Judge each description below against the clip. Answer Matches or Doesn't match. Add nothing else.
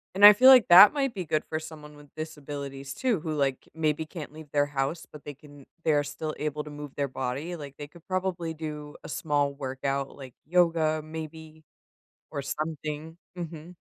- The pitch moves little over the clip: Matches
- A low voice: Doesn't match